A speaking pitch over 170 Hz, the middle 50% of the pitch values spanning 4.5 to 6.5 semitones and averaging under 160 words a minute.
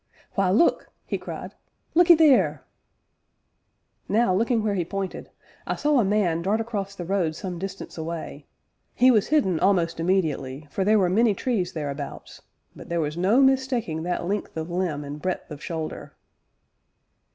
No: high, 190 Hz; average, 4.8 semitones; average, 165 wpm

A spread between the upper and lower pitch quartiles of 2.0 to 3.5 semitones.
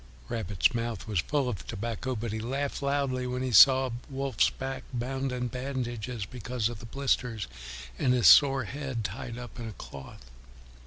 Yes: average, 2.8 semitones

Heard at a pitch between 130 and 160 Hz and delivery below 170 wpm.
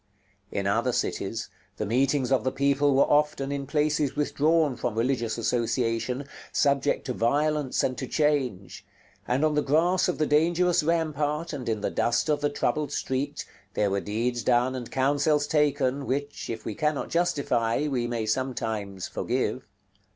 Yes: medium, 140 Hz; average, 160 wpm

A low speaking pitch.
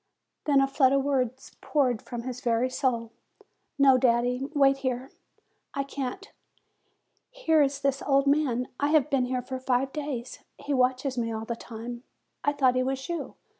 No: very high, 265 Hz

